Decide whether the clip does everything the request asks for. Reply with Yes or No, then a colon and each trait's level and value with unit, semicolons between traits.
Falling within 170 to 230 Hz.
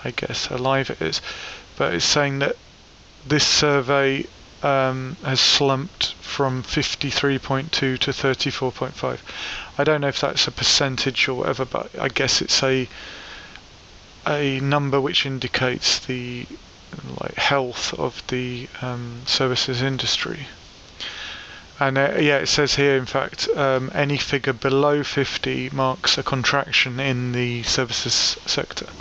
No: low, 135 Hz